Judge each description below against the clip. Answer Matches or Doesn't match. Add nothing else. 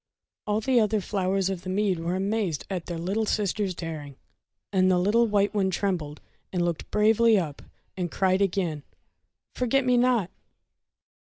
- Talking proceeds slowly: Doesn't match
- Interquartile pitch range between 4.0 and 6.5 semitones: Doesn't match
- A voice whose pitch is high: Matches